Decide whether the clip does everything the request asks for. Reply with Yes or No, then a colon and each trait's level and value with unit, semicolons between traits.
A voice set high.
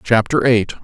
No: low, 115 Hz